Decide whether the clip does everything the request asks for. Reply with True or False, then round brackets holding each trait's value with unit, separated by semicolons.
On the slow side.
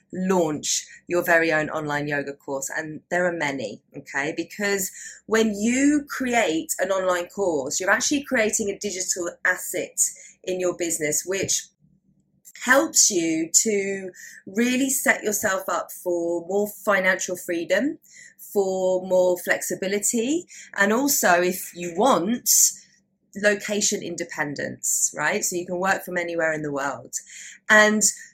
True (130 wpm)